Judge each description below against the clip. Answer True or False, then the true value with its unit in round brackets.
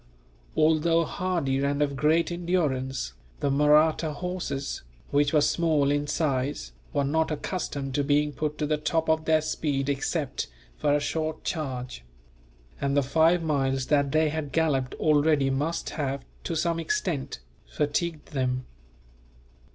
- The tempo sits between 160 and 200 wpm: False (145 wpm)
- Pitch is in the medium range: True (150 Hz)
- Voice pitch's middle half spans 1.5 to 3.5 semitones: True (2.5 semitones)